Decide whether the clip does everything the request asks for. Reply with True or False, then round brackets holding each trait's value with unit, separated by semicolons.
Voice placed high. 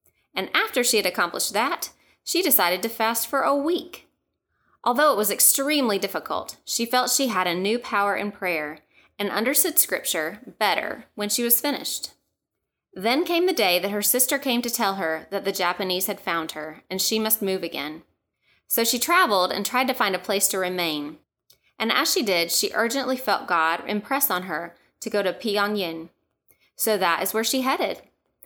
True (205 Hz)